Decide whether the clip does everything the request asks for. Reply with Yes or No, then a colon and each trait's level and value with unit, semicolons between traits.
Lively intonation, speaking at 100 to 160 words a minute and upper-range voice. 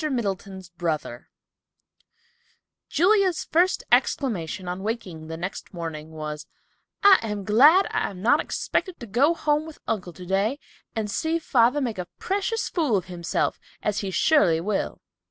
Yes: wide, 9.0 semitones; average, 145 wpm; high, 210 Hz